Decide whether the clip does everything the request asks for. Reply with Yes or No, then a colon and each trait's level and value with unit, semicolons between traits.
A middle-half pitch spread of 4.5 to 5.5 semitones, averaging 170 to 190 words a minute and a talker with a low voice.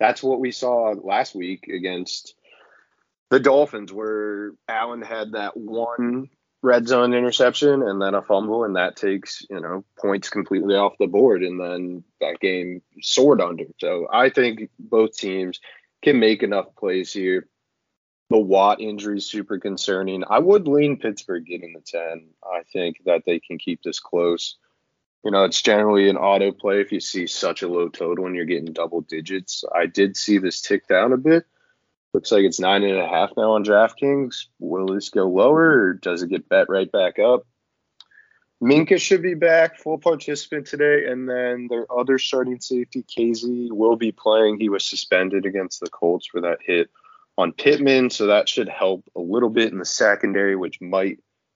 Yes: average, 5.2 semitones; average, 185 wpm; low, 110 Hz